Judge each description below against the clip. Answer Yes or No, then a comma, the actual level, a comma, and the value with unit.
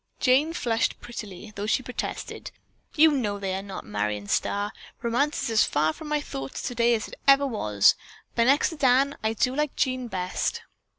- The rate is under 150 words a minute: No, average, 185 wpm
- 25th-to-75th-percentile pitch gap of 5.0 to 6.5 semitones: Yes, wide, 5.5 semitones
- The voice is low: No, high, 235 Hz